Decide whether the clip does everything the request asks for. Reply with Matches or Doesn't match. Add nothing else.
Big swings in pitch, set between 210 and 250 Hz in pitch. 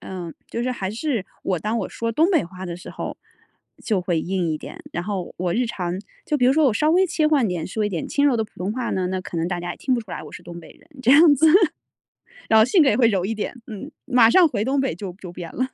Matches